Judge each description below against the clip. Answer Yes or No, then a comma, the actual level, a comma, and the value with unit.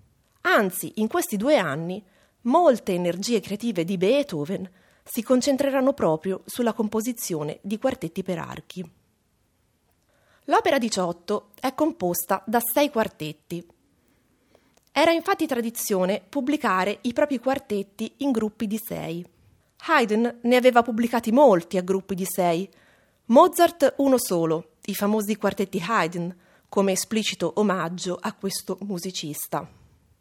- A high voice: Yes, high, 205 Hz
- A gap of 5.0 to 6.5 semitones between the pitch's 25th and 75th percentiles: Yes, average, 5.3 semitones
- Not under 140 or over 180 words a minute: No, slow, 115 wpm